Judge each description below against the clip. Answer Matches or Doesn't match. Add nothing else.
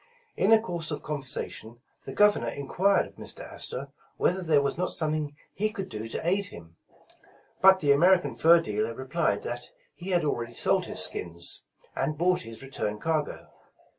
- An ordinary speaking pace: Matches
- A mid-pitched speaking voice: Matches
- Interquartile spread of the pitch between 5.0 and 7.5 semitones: Matches